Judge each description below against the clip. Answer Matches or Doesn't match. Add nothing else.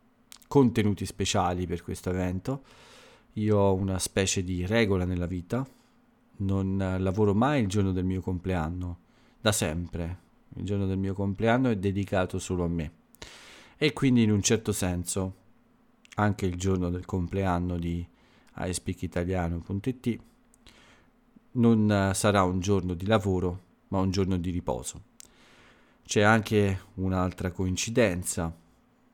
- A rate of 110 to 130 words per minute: Matches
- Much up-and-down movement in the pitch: Doesn't match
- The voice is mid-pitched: Doesn't match